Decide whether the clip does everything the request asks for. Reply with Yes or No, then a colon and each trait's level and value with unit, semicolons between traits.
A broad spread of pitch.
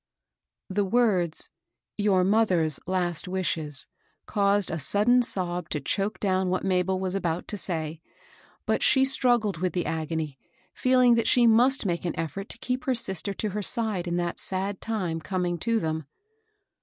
No: average, 4.0 semitones